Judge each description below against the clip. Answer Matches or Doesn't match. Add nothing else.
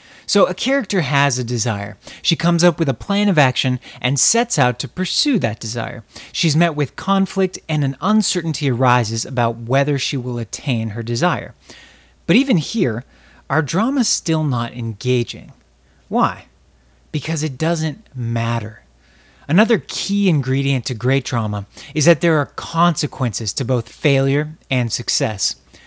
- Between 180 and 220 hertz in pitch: Doesn't match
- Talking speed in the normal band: Matches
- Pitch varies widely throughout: Matches